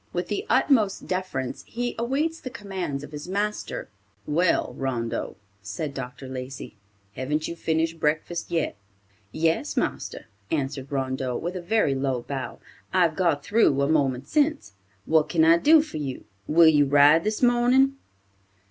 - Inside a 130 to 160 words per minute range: Yes, average, 150 wpm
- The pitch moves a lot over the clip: Yes, wide, 6.5 semitones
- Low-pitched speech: No, medium, 160 Hz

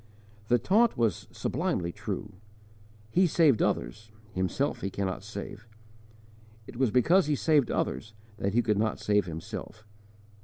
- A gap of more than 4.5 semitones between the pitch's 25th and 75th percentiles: Yes, average, 5.3 semitones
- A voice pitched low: Yes, low, 110 Hz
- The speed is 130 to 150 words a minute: Yes, average, 140 wpm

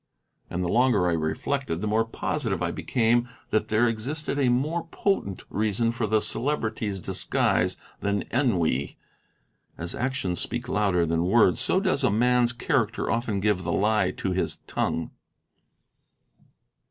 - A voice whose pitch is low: Yes, low, 110 Hz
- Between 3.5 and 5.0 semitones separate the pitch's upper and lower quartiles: Yes, average, 4.6 semitones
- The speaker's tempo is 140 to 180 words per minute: Yes, average, 145 wpm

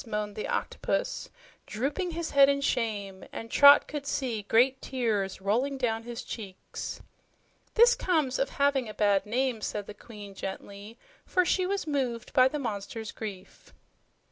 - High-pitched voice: Yes, high, 235 Hz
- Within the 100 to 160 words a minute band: Yes, average, 155 wpm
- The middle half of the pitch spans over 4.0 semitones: Yes, average, 5.0 semitones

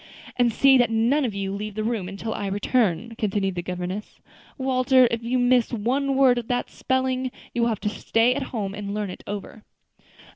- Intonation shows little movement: No, average, 3.9 semitones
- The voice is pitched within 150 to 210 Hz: No, high, 230 Hz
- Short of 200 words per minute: No, fast, 205 wpm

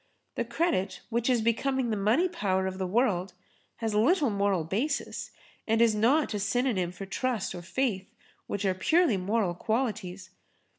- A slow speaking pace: No, average, 165 wpm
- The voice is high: Yes, high, 215 Hz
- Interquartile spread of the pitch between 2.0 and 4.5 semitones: No, average, 4.9 semitones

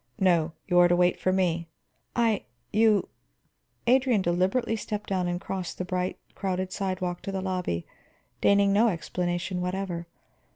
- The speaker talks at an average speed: Yes, average, 155 wpm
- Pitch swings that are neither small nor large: No, narrow, 2.2 semitones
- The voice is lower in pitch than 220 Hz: Yes, medium, 185 Hz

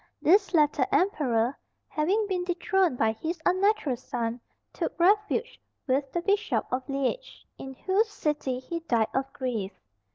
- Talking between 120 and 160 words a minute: Yes, average, 140 wpm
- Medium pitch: No, very high, 305 Hz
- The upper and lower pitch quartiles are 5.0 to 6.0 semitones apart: No, wide, 6.9 semitones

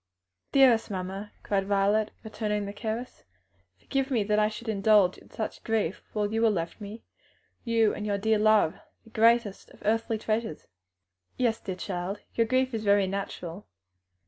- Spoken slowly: No, average, 165 wpm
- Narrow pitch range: Yes, narrow, 2.1 semitones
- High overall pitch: Yes, high, 215 Hz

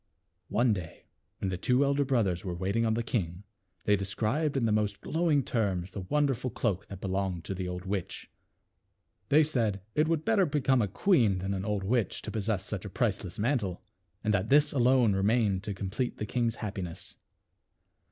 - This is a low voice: Yes, low, 105 Hz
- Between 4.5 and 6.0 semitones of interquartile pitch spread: Yes, average, 4.9 semitones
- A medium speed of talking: Yes, average, 190 wpm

